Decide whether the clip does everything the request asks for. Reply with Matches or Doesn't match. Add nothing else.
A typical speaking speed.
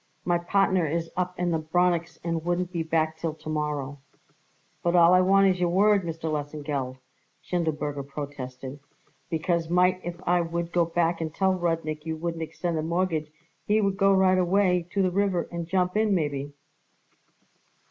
Matches